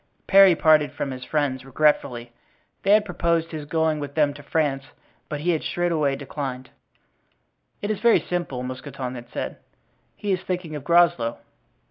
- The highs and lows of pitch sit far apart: No, average, 4.3 semitones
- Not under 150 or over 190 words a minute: Yes, average, 160 wpm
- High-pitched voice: No, medium, 150 Hz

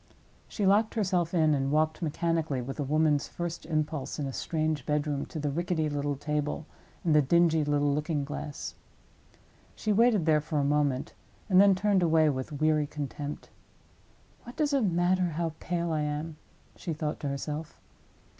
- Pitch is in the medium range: Yes, medium, 155 Hz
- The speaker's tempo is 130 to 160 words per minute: No, average, 170 wpm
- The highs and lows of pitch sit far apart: No, average, 2.7 semitones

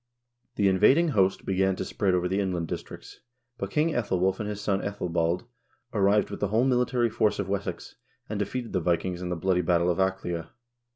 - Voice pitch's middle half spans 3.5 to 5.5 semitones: No, average, 2.8 semitones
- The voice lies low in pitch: Yes, very low, 95 Hz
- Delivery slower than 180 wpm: No, average, 190 wpm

